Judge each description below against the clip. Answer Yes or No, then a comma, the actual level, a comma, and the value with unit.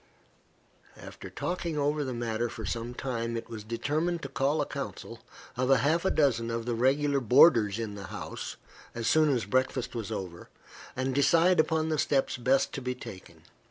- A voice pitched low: Yes, low, 130 Hz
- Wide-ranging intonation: No, average, 4.1 semitones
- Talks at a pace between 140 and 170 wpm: No, average, 180 wpm